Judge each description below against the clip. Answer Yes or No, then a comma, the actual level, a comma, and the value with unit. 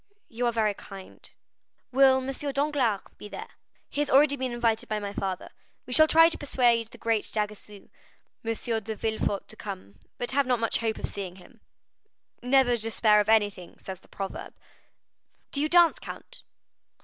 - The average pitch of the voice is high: Yes, high, 230 Hz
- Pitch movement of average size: Yes, average, 4.3 semitones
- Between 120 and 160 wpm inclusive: No, average, 175 wpm